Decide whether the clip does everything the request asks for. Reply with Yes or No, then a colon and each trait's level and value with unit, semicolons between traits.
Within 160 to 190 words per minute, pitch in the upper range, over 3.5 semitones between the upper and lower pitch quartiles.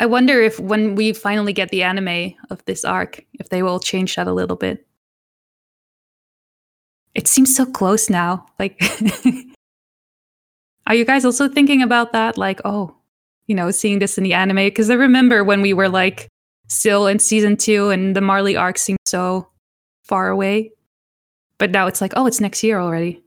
No: average, 180 wpm; high, 200 Hz; average, 3.1 semitones